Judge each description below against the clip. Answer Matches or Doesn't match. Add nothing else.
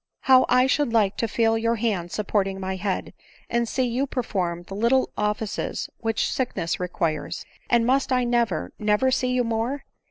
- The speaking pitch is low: Doesn't match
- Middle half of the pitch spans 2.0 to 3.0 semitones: Doesn't match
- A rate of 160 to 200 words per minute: Matches